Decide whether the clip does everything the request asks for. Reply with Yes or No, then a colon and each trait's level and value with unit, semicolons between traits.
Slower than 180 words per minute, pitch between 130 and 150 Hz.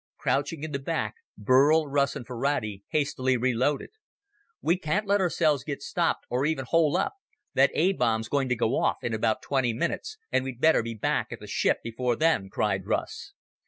No: average, 190 wpm; medium, 140 Hz